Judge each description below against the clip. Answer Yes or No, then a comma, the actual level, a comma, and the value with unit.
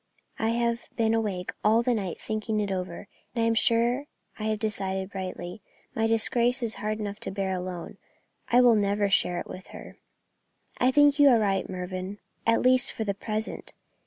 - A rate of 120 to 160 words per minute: No, average, 190 wpm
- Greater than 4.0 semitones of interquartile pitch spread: No, average, 3.3 semitones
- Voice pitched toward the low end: No, high, 215 Hz